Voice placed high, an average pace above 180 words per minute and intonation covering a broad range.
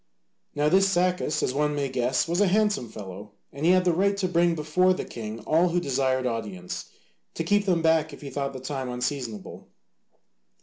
No: medium, 150 Hz; average, 200 wpm; wide, 6.0 semitones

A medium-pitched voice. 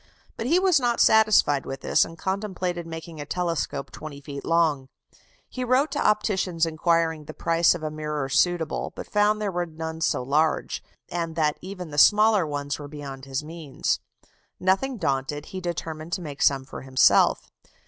Yes: medium, 165 Hz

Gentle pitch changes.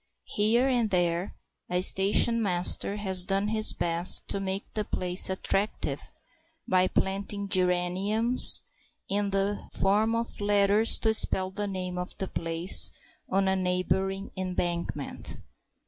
Yes: narrow, 2.1 semitones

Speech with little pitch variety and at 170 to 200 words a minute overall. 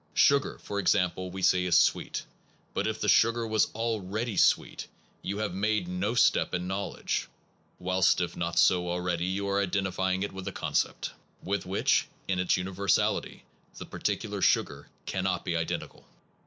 No: narrow, 1.9 semitones; average, 160 wpm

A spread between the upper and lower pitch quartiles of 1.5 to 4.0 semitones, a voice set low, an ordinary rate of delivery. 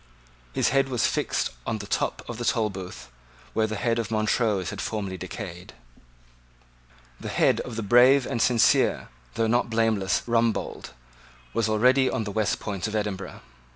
Yes: narrow, 2.6 semitones; low, 110 Hz; average, 160 wpm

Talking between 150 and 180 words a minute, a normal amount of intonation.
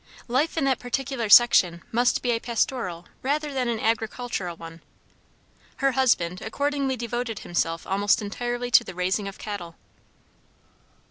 No: average, 140 wpm; average, 4.9 semitones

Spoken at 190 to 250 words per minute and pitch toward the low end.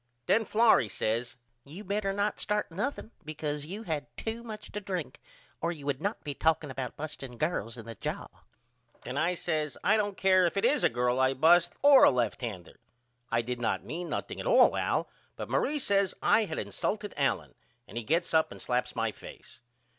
No: average, 200 wpm; medium, 160 Hz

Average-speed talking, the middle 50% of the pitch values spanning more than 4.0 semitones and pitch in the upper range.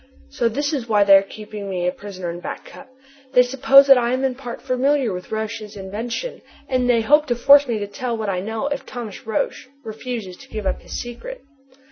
No: fast, 220 wpm; average, 4.4 semitones; high, 235 Hz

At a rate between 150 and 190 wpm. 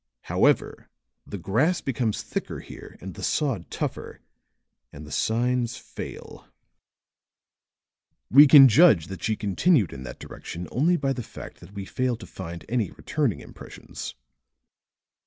No: average, 140 wpm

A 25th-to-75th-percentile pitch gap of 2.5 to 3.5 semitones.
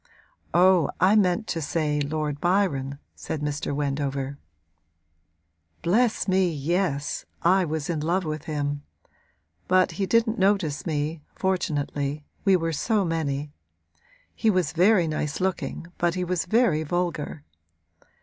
No: average, 4.1 semitones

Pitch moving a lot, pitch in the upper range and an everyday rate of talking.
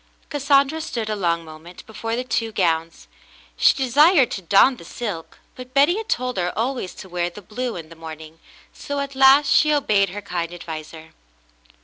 Yes: wide, 8.0 semitones; high, 215 Hz; average, 185 wpm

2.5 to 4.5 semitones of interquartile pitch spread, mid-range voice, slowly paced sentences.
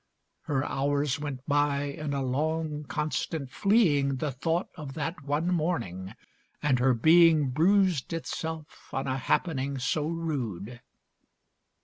Yes: average, 3.2 semitones; medium, 145 Hz; slow, 125 wpm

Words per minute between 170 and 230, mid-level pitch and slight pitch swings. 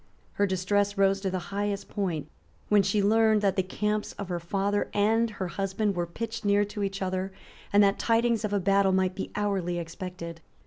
No: average, 195 wpm; high, 200 Hz; narrow, 1.7 semitones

